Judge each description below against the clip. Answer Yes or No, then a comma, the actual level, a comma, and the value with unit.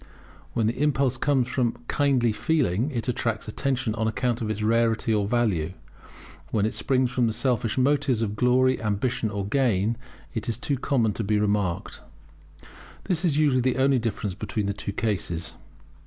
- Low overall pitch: Yes, low, 115 Hz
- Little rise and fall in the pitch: No, average, 3.3 semitones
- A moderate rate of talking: Yes, average, 170 wpm